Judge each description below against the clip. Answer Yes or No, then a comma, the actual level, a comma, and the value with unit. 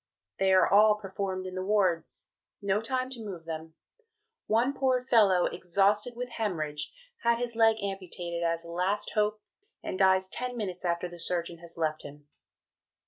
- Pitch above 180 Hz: Yes, high, 190 Hz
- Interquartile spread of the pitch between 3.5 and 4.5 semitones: Yes, average, 4.1 semitones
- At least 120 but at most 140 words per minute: No, average, 165 wpm